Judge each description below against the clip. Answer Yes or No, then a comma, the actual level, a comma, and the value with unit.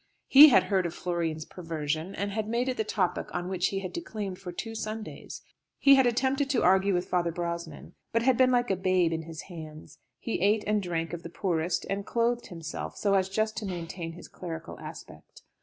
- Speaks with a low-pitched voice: No, medium, 185 Hz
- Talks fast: Yes, fast, 210 wpm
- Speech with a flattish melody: No, average, 4.4 semitones